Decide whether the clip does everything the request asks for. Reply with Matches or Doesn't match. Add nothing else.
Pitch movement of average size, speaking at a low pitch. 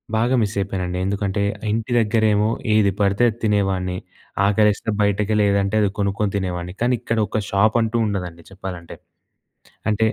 Doesn't match